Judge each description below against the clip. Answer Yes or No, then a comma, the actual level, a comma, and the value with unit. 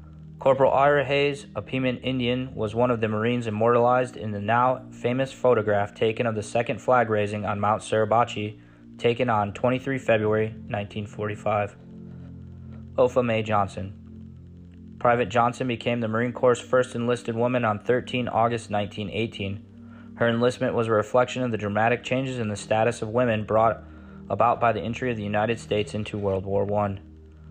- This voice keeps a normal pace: Yes, average, 155 wpm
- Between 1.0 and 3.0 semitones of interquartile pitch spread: Yes, average, 2.7 semitones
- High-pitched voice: No, low, 115 Hz